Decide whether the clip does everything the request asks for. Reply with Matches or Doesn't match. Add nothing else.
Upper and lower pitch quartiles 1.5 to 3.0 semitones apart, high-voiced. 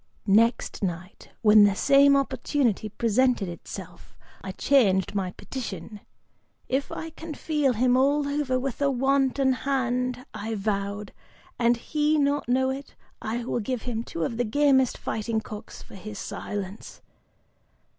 Doesn't match